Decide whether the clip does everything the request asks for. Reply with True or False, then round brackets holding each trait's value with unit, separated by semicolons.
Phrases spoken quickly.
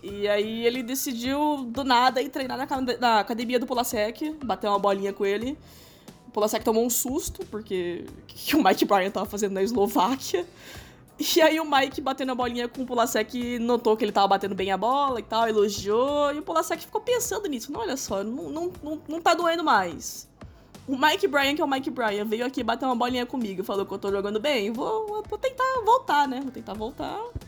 True (215 wpm)